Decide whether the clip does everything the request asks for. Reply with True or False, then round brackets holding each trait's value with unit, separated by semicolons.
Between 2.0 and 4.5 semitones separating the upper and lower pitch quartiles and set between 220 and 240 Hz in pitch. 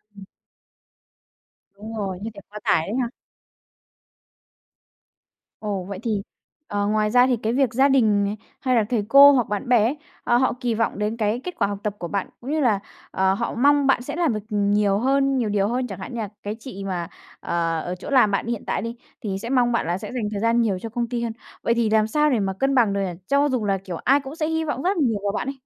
True (4.1 semitones; 225 Hz)